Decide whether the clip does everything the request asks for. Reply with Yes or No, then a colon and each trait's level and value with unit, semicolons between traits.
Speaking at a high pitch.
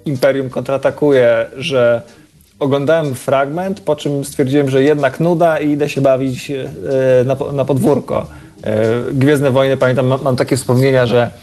No: low, 135 Hz